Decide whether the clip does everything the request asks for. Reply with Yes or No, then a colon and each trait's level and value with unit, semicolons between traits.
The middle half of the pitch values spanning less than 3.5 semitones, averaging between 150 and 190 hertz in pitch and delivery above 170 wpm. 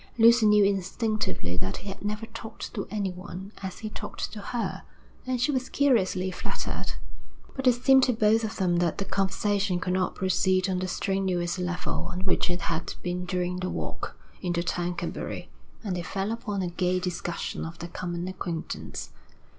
Yes: average, 3.0 semitones; medium, 185 Hz; average, 180 wpm